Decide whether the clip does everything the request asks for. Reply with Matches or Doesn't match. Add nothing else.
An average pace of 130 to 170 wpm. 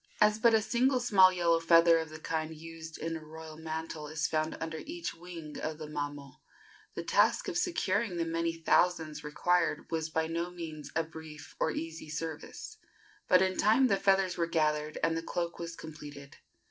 Doesn't match